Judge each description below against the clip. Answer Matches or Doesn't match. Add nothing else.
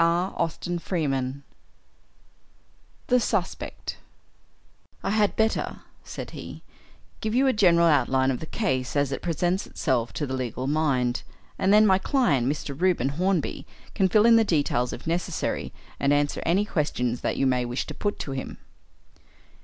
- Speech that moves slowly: Doesn't match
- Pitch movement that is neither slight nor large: Doesn't match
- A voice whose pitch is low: Doesn't match